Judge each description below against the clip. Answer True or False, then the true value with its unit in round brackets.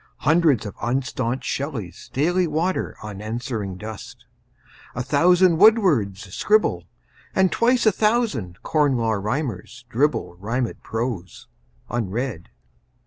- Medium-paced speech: False (105 wpm)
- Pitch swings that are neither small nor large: False (7.5 semitones)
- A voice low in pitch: True (125 Hz)